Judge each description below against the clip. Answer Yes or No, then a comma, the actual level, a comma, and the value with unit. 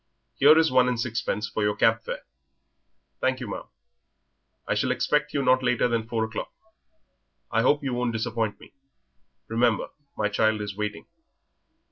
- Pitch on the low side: Yes, low, 115 Hz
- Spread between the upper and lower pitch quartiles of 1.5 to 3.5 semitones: Yes, average, 2.7 semitones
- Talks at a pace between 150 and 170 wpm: Yes, average, 160 wpm